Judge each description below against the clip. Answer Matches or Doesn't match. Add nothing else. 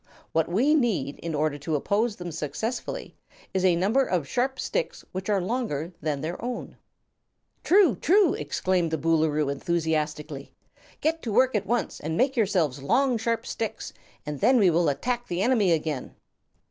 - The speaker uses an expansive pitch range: Matches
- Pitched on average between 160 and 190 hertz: Matches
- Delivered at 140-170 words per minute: Matches